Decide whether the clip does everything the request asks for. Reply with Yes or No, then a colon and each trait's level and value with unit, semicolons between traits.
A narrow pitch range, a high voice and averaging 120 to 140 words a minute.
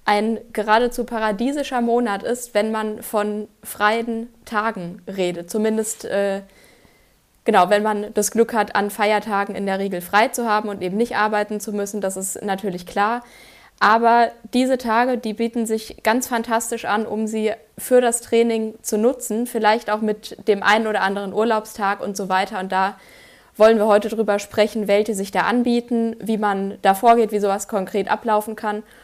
No: narrow, 2.1 semitones; high, 215 Hz; average, 175 wpm